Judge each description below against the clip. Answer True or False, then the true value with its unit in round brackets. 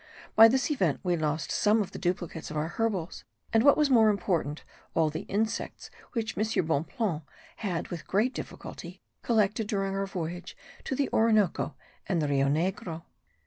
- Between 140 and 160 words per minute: False (170 wpm)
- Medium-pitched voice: False (195 Hz)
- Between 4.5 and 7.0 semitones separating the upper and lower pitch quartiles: True (5.3 semitones)